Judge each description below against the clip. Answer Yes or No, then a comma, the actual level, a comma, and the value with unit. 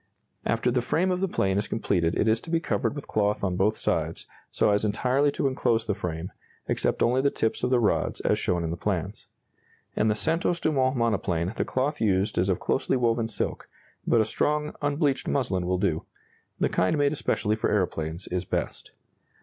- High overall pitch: No, low, 110 Hz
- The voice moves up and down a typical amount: No, wide, 6.3 semitones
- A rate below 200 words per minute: No, fast, 205 wpm